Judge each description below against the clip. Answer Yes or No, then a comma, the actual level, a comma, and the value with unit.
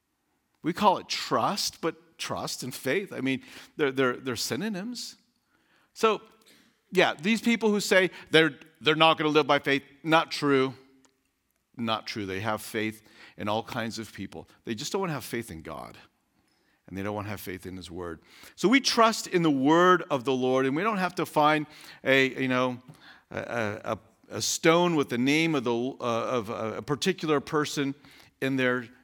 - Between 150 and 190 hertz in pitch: No, low, 135 Hz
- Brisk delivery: No, average, 190 wpm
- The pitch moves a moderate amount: No, wide, 5.7 semitones